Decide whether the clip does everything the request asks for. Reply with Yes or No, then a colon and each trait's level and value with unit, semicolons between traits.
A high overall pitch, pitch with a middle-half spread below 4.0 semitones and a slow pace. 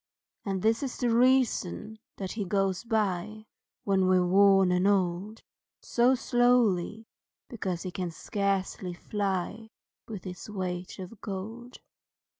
Yes: high, 200 Hz; average, 3.2 semitones; slow, 125 wpm